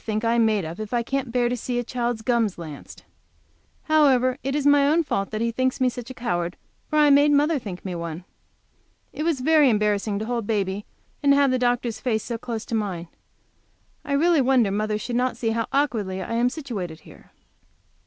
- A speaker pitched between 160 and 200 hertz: No, high, 235 Hz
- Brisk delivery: Yes, fast, 215 wpm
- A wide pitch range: No, average, 4.3 semitones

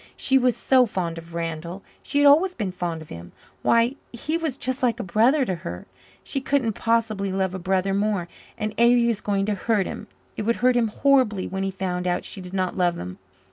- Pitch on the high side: Yes, high, 205 Hz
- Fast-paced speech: Yes, fast, 220 wpm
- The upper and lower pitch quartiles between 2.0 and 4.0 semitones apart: No, average, 5.1 semitones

